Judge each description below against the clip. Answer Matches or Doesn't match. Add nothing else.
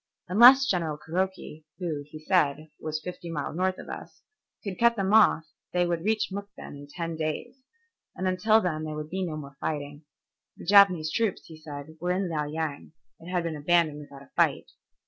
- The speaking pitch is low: Doesn't match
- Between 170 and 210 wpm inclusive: Matches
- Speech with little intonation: Doesn't match